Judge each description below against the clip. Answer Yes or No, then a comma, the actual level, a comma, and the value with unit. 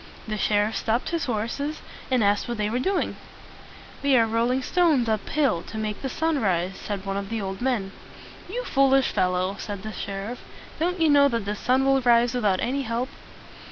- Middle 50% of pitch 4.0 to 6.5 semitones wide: Yes, average, 4.7 semitones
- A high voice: Yes, high, 235 Hz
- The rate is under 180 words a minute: No, average, 195 wpm